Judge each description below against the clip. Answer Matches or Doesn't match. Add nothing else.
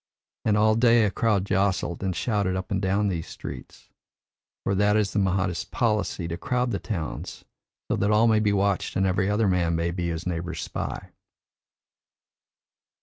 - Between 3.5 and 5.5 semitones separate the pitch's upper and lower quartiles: Doesn't match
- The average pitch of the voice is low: Matches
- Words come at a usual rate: Matches